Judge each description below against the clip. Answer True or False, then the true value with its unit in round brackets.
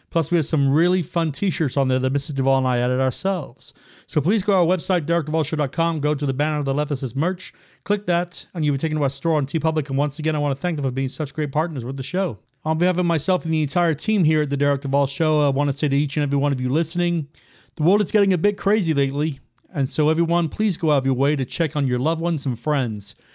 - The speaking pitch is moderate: True (155 Hz)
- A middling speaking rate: False (285 wpm)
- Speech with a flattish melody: False (3.4 semitones)